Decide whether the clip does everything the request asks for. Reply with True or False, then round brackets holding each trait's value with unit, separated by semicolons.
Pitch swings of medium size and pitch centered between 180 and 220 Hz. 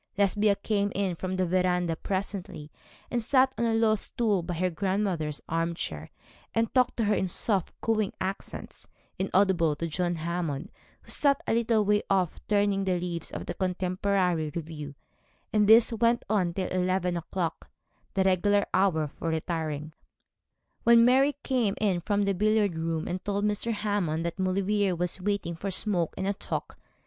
True (3.4 semitones; 190 Hz)